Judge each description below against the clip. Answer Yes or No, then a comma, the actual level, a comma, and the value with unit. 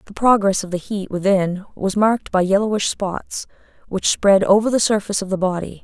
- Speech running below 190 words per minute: No, average, 195 wpm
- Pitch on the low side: No, high, 200 Hz